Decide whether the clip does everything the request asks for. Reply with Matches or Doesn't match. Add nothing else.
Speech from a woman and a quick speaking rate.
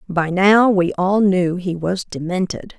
Doesn't match